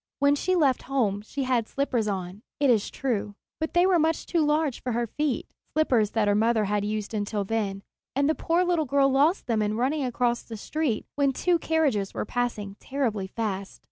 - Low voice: No, high, 245 Hz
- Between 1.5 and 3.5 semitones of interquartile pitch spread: No, wide, 5.6 semitones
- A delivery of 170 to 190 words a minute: No, fast, 205 wpm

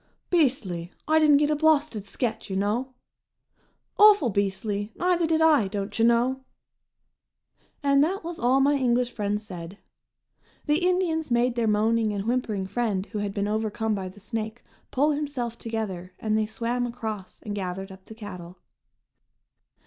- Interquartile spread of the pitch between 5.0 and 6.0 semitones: Yes, wide, 5.4 semitones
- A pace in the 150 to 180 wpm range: Yes, average, 155 wpm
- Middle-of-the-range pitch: No, high, 230 Hz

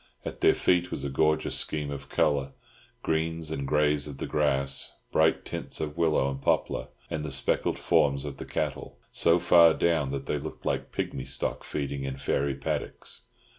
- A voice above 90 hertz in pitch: No, very low, 75 Hz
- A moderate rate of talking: Yes, average, 180 wpm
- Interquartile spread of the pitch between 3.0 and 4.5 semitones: No, narrow, 2.4 semitones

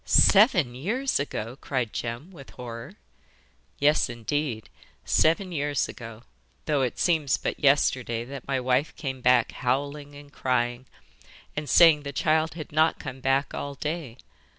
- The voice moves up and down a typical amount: Yes, average, 3.4 semitones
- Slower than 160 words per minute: Yes, average, 145 wpm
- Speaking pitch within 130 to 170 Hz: Yes, medium, 140 Hz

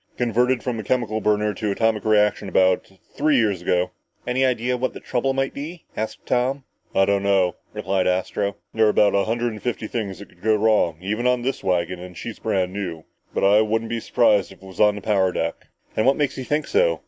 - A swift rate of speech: Yes, fast, 220 wpm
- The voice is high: No, low, 110 Hz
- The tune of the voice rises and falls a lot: No, average, 4.1 semitones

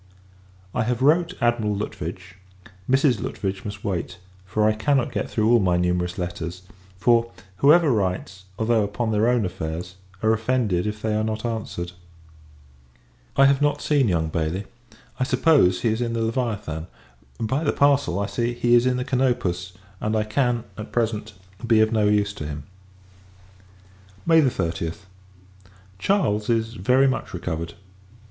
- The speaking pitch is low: Yes, low, 110 Hz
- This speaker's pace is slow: No, average, 155 wpm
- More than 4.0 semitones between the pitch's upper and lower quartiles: Yes, average, 5.0 semitones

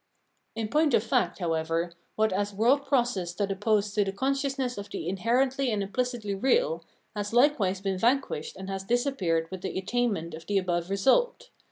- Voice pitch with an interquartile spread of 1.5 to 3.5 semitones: No, average, 4.8 semitones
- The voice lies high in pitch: Yes, high, 205 Hz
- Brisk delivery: No, average, 175 wpm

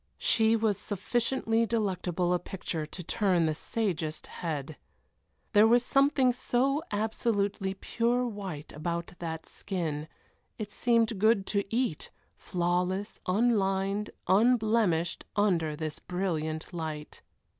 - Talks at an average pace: No, slow, 115 wpm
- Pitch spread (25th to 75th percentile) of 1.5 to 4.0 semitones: No, average, 4.8 semitones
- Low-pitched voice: No, high, 195 Hz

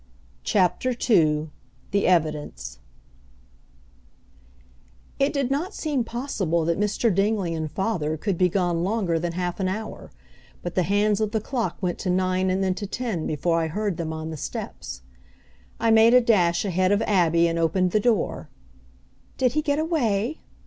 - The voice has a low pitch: No, high, 190 Hz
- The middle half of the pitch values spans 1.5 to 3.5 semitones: No, average, 4.8 semitones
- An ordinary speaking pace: Yes, average, 165 wpm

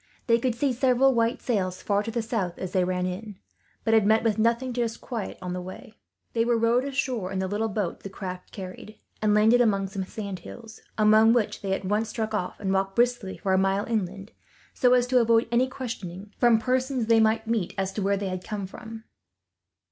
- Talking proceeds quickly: Yes, fast, 225 wpm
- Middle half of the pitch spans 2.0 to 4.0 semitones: Yes, average, 3.4 semitones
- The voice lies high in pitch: Yes, high, 220 Hz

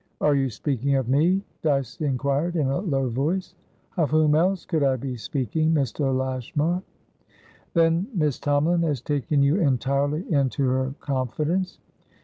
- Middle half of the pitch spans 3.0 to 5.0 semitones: Yes, average, 3.4 semitones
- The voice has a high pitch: No, medium, 145 Hz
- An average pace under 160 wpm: Yes, average, 145 wpm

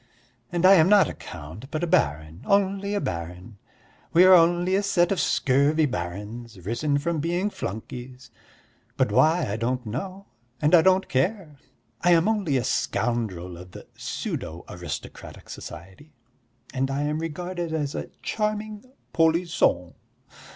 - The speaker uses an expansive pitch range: Yes, wide, 8.1 semitones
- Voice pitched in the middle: Yes, medium, 150 Hz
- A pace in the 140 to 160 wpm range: Yes, average, 150 wpm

